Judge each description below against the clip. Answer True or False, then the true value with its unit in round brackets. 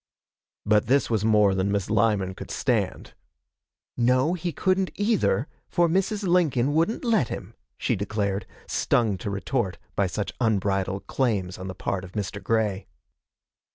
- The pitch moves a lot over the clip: True (6.7 semitones)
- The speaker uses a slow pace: False (150 wpm)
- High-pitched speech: False (110 Hz)